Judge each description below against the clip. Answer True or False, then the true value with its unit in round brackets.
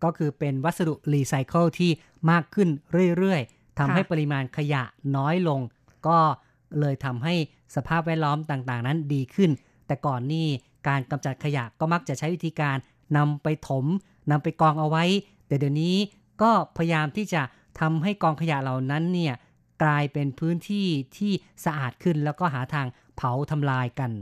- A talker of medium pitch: True (150 Hz)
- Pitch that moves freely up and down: False (3.5 semitones)